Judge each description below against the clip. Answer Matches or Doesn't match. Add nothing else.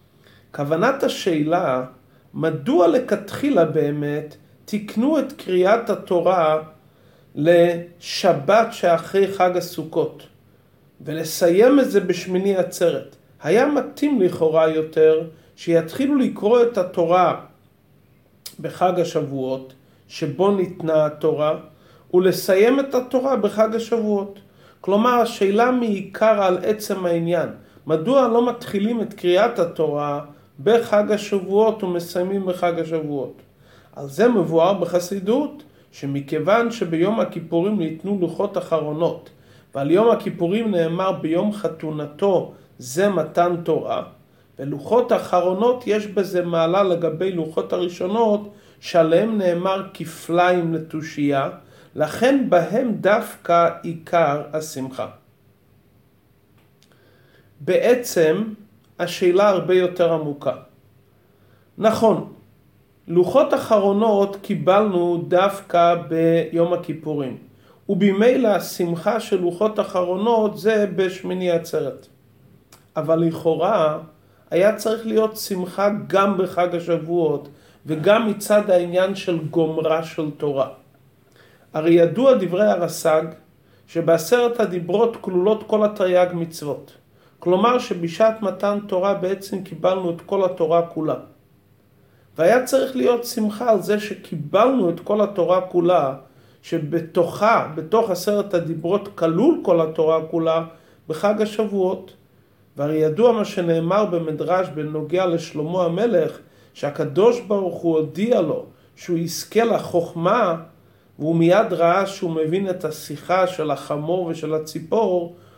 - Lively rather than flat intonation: Doesn't match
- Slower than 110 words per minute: Matches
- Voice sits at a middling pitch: Matches